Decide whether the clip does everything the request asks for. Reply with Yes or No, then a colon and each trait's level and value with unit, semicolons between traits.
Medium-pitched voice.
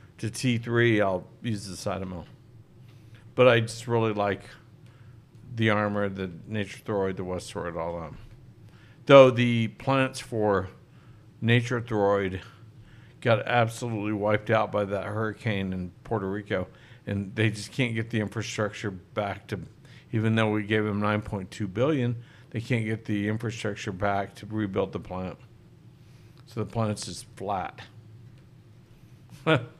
No: low, 110 Hz